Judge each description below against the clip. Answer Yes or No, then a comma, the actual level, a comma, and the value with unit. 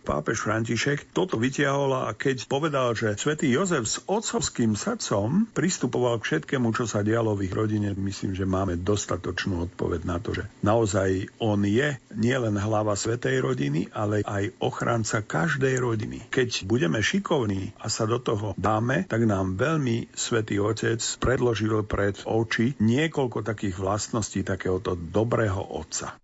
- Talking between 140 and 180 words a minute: Yes, average, 145 wpm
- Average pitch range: Yes, average, 3.7 semitones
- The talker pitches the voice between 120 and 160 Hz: No, low, 110 Hz